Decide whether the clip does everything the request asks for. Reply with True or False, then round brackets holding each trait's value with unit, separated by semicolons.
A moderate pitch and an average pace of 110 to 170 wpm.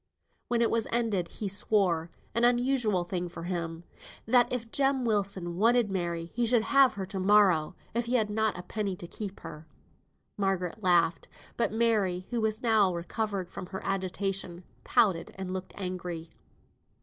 False (195 Hz; 165 wpm)